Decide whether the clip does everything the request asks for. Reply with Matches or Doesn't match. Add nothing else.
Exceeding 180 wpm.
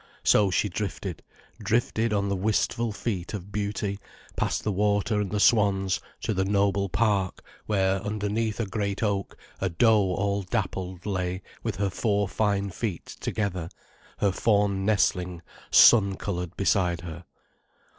Doesn't match